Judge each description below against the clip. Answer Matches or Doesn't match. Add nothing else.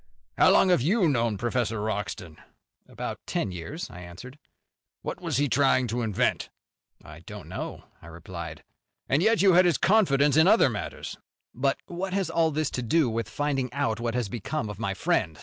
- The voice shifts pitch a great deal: Matches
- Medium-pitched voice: Doesn't match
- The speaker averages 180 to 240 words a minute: Matches